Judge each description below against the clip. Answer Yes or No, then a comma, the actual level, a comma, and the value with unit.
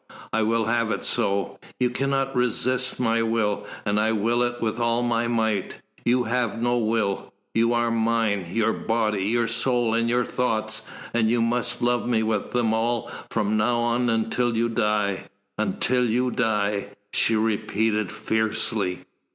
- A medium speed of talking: Yes, average, 160 wpm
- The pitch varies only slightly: Yes, narrow, 1.8 semitones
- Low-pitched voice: Yes, low, 115 Hz